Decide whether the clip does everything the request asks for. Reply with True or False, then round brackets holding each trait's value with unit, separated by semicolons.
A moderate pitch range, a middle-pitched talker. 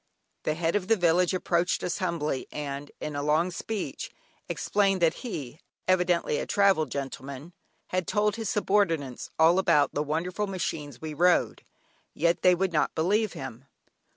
True (3.9 semitones; 170 Hz)